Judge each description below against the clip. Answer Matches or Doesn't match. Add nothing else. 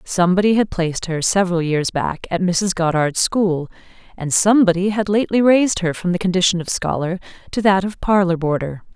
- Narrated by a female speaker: Matches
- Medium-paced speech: Matches